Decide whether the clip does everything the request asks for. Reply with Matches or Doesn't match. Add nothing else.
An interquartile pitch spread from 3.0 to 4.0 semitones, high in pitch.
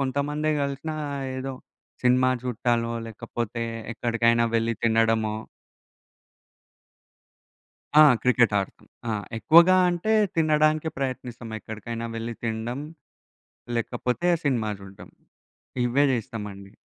Doesn't match